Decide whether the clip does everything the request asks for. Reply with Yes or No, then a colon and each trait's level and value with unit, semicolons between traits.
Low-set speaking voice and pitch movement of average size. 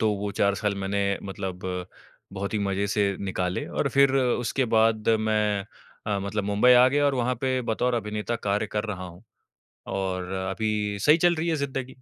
Yes: low, 105 Hz; average, 4.0 semitones